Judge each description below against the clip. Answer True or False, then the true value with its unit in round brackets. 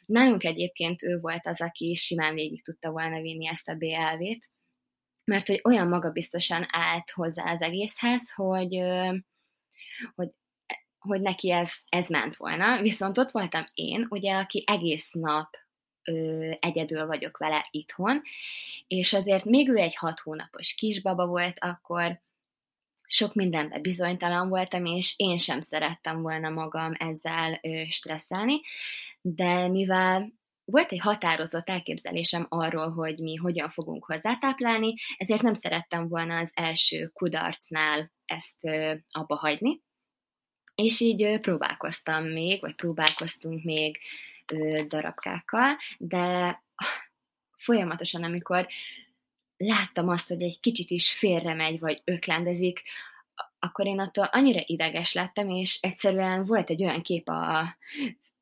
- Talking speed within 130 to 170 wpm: False (120 wpm)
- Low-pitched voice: False (175 Hz)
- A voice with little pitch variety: False (3.5 semitones)